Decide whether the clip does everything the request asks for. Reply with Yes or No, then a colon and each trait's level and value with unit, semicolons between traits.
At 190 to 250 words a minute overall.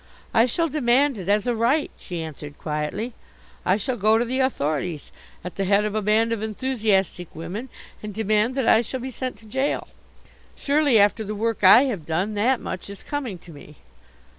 Yes: average, 195 wpm